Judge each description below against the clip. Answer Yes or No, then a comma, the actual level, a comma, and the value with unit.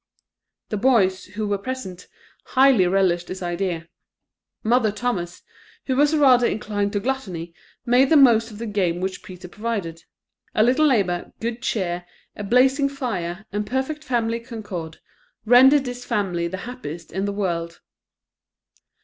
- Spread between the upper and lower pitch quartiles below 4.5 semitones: No, average, 5.3 semitones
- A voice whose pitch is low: No, high, 210 Hz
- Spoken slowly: No, average, 145 wpm